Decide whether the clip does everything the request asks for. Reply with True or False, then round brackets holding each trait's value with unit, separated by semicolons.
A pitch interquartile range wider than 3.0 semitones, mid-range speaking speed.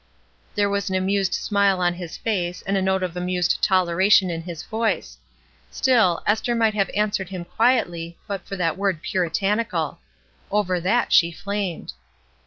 False (2.7 semitones; 160 wpm)